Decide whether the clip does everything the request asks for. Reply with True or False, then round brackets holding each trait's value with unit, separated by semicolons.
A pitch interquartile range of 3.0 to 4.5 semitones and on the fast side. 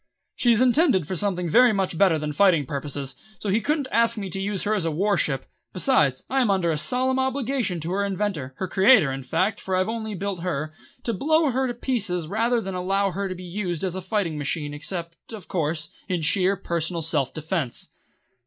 False (4.9 semitones; 215 wpm)